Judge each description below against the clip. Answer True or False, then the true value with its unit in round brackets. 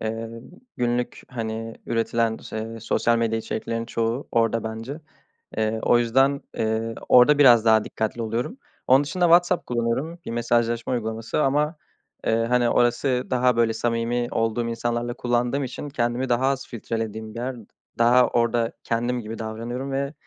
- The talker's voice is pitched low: True (120 Hz)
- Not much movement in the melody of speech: True (1.9 semitones)